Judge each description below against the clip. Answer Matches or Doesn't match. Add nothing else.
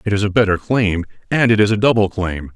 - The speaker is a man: Matches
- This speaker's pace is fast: Matches